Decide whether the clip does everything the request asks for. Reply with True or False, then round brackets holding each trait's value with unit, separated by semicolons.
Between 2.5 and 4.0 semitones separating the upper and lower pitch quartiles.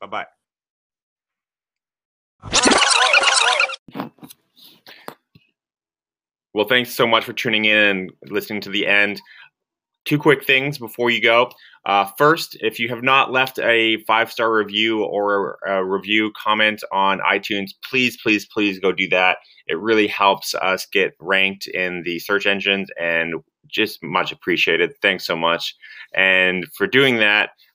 True (2.8 semitones)